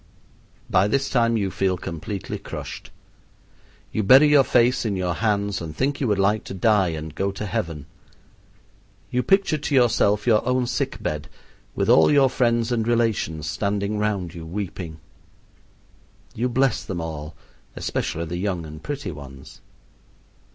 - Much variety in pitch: Yes, wide, 5.9 semitones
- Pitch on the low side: Yes, low, 100 Hz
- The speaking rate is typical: Yes, average, 155 wpm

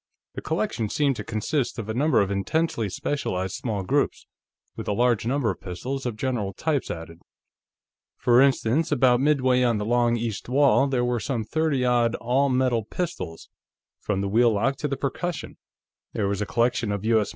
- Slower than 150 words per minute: No, average, 175 wpm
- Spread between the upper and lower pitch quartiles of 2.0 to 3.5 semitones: No, average, 4.3 semitones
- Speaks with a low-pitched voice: Yes, low, 120 Hz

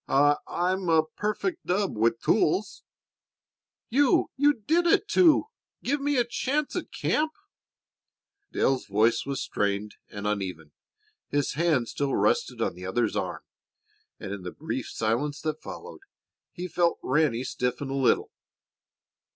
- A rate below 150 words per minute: Yes, average, 140 wpm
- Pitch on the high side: No, medium, 145 Hz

